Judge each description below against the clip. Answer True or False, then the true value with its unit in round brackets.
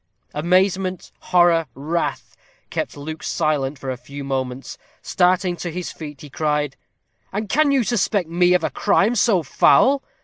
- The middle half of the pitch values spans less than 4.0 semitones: False (4.3 semitones)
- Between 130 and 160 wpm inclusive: True (150 wpm)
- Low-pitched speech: False (170 Hz)